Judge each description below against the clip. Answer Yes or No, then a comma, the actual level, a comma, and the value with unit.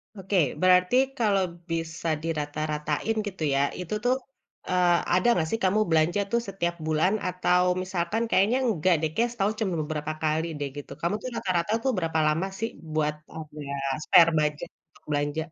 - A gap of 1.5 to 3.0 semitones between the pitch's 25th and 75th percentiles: No, average, 3.7 semitones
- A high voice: No, medium, 170 Hz